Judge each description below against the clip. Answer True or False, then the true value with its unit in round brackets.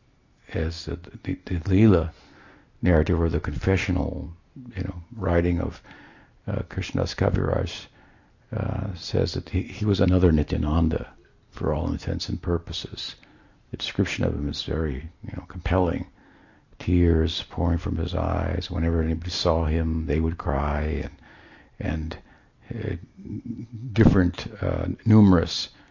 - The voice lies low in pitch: True (90 Hz)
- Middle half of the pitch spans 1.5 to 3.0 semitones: True (2.7 semitones)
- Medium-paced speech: False (130 wpm)